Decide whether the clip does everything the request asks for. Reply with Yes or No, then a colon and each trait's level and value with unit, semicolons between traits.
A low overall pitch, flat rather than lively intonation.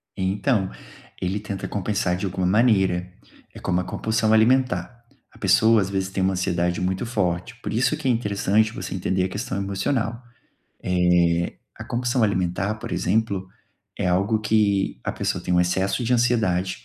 No: low, 100 Hz; average, 3.4 semitones